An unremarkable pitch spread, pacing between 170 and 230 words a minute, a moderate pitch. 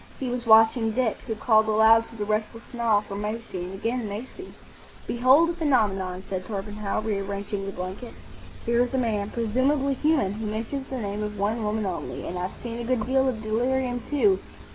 No: average, 3.2 semitones; average, 185 wpm; high, 220 Hz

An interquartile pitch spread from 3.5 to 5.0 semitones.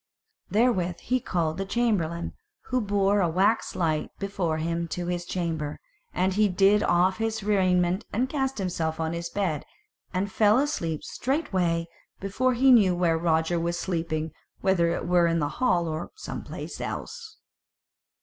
Yes: average, 3.8 semitones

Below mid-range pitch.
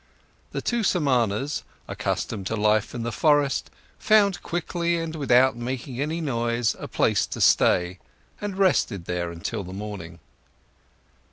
Yes: low, 125 Hz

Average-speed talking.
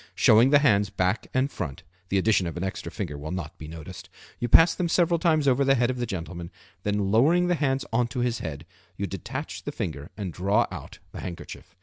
No: fast, 225 wpm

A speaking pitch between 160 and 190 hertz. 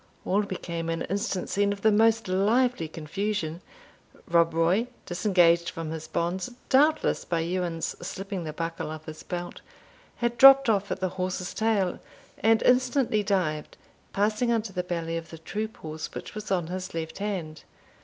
Yes: medium, 185 Hz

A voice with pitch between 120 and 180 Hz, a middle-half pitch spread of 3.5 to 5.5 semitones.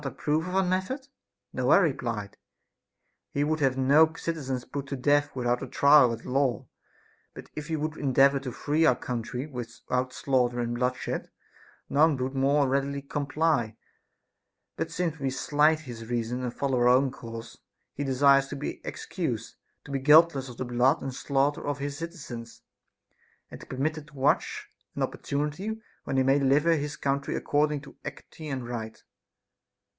No: medium, 140 Hz; average, 2.8 semitones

